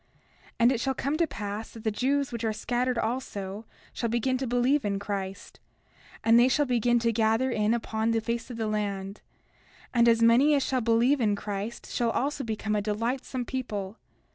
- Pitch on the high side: Yes, high, 230 Hz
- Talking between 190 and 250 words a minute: Yes, average, 195 wpm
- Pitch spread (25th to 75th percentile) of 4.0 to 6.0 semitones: No, average, 3.0 semitones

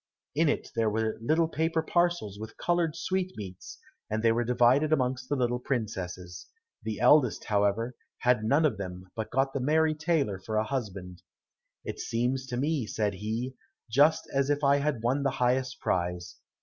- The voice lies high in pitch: No, low, 125 Hz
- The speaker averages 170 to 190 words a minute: Yes, average, 175 wpm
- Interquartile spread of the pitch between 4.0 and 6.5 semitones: Yes, average, 5.2 semitones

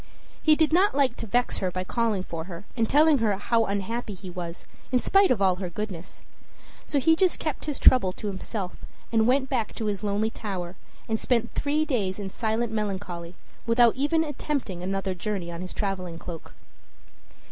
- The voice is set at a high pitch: Yes, high, 215 Hz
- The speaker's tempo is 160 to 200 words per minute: Yes, average, 185 wpm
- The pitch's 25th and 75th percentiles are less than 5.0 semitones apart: No, wide, 5.4 semitones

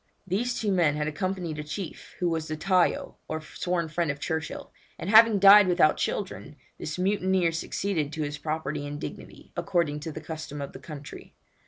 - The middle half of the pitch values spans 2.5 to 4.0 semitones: Yes, average, 3.7 semitones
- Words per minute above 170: Yes, average, 185 wpm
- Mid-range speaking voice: Yes, medium, 165 Hz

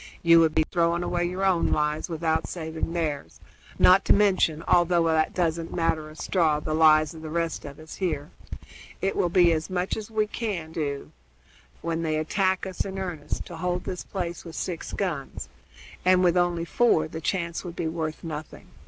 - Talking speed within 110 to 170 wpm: No, average, 190 wpm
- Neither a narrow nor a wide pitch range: No, narrow, 2.3 semitones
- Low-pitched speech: No, medium, 170 Hz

